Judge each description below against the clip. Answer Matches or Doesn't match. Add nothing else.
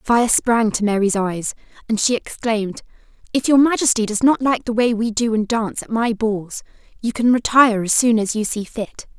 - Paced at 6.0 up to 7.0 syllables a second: Doesn't match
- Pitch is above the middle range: Matches